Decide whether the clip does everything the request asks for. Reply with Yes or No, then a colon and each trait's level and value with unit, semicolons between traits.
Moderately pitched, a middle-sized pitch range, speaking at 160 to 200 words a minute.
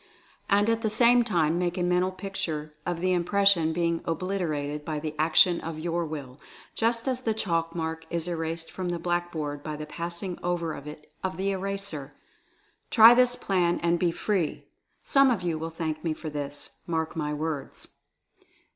Yes: medium, 170 Hz; average, 3.2 semitones; average, 175 wpm